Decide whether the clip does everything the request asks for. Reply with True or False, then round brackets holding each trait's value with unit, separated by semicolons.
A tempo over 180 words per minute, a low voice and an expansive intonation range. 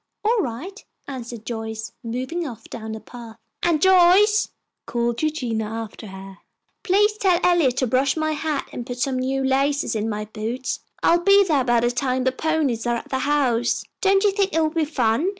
False (190 wpm; 265 Hz; 6.0 semitones)